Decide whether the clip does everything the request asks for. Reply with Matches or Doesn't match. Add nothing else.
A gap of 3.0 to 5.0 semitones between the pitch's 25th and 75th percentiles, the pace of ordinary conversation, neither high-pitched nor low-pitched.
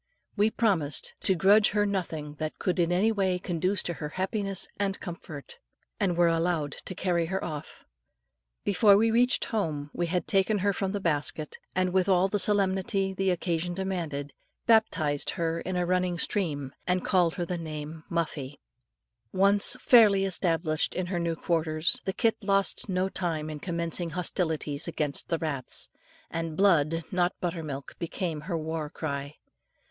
Matches